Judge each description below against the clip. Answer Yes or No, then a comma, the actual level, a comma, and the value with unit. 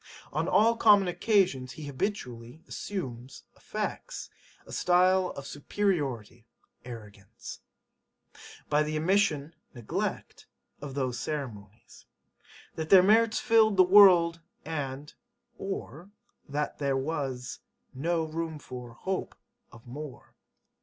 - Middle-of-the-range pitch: Yes, medium, 155 Hz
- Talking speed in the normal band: No, slow, 105 wpm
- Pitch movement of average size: No, wide, 6.3 semitones